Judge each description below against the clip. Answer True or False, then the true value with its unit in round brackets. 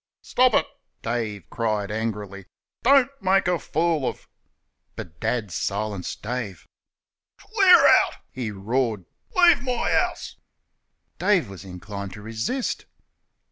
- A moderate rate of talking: False (130 wpm)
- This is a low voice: True (110 Hz)